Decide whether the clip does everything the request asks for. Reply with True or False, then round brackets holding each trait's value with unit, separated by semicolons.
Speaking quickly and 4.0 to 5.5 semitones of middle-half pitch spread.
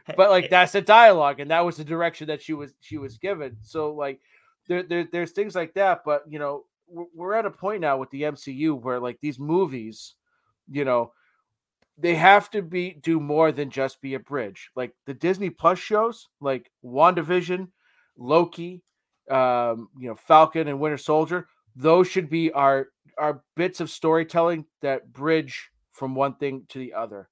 False (180 wpm; 4.5 semitones)